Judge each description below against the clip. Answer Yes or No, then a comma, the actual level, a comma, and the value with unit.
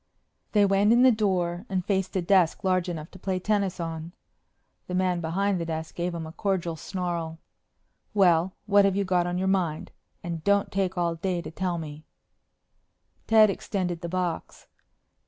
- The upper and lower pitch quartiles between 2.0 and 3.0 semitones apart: Yes, narrow, 2.4 semitones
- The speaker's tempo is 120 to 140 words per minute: No, average, 175 wpm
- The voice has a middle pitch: Yes, medium, 180 Hz